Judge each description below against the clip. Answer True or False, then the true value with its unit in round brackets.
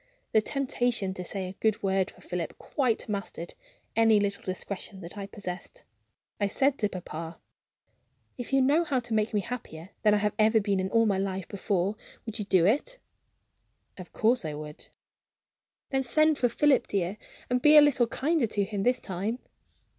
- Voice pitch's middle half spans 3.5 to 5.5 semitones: True (4.5 semitones)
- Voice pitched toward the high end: True (210 Hz)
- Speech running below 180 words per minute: False (185 wpm)